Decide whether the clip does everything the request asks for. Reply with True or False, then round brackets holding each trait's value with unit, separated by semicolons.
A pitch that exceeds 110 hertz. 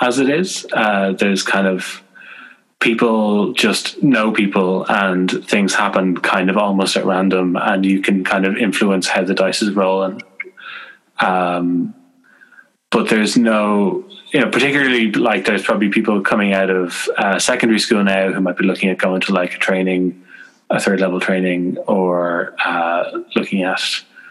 False (95 Hz)